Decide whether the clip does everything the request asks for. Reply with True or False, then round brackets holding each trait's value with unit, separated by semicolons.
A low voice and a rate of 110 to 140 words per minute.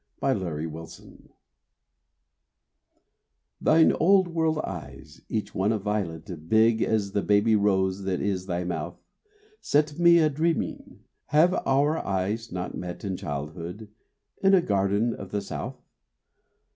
True (100 Hz; 135 wpm)